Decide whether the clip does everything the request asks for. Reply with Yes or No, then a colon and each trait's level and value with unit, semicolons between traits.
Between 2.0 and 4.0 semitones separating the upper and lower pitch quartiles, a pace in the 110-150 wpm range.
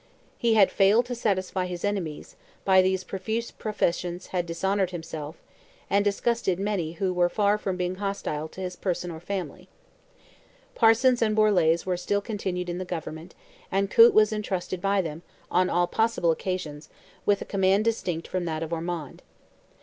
No: average, 2.8 semitones; average, 165 wpm